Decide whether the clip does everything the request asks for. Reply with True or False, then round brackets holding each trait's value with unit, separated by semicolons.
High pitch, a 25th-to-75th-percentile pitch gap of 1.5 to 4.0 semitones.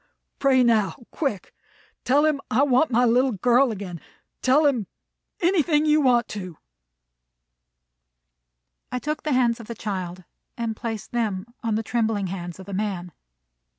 False (235 Hz; 4.8 semitones)